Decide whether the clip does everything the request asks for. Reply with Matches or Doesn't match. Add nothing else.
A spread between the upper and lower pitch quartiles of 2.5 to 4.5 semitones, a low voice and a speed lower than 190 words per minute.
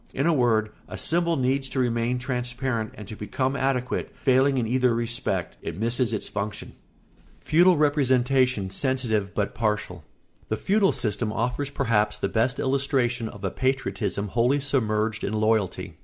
Matches